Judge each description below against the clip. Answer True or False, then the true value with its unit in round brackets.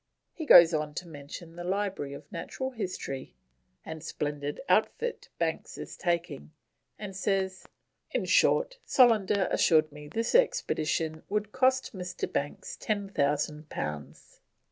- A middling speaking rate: False (125 wpm)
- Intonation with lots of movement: True (5.7 semitones)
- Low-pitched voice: False (175 Hz)